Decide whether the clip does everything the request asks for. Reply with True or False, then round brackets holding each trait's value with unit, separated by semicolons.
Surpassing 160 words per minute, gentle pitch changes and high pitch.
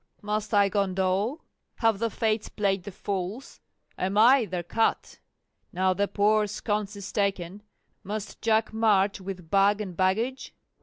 False (145 wpm; 2.2 semitones; 205 Hz)